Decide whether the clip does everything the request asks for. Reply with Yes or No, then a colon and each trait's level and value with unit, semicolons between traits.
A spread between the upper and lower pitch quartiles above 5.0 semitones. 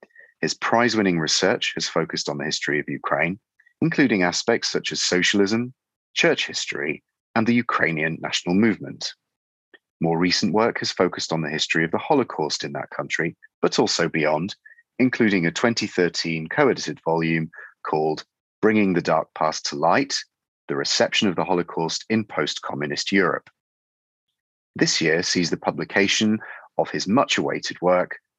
Yes: wide, 5.6 semitones